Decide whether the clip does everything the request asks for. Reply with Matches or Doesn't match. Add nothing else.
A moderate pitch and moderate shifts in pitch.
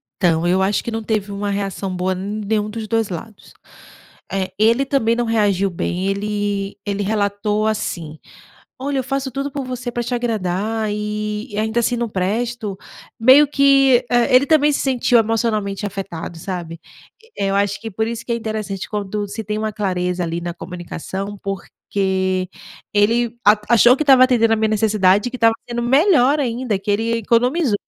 Doesn't match